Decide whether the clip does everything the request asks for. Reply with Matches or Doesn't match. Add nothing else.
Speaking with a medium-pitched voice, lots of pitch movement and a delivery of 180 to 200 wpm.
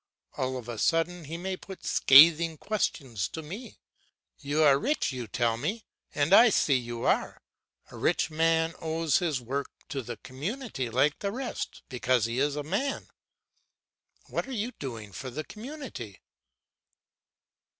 Doesn't match